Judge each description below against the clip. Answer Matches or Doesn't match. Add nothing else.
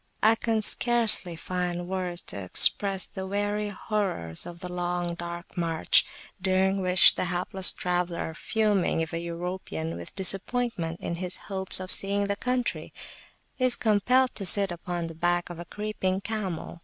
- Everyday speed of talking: Matches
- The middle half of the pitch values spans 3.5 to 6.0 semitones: Doesn't match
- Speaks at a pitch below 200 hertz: Matches